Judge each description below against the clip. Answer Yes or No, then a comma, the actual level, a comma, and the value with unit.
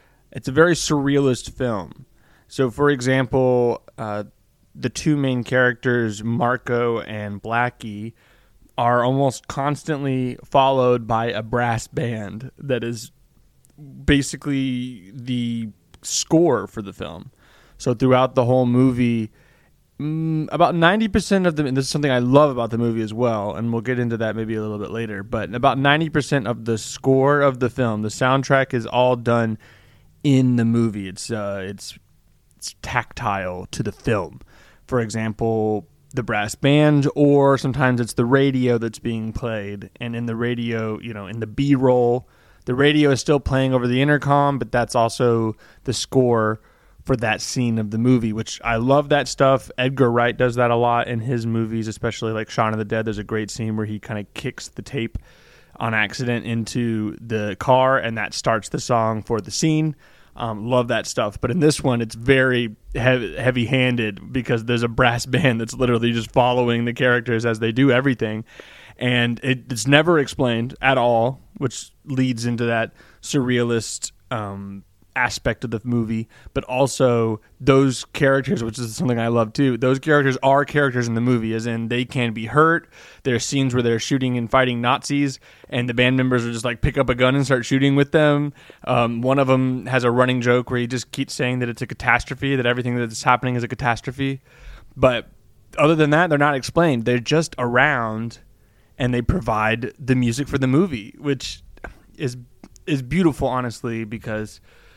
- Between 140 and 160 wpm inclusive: No, average, 180 wpm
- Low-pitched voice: Yes, low, 125 Hz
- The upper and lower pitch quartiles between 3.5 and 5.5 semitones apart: No, average, 2.8 semitones